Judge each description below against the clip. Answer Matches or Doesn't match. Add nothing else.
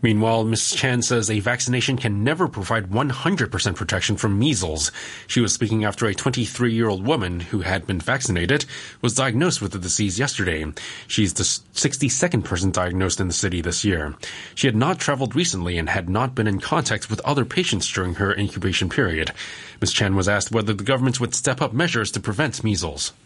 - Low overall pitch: Matches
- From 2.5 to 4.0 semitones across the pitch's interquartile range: Doesn't match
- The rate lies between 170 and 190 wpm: Matches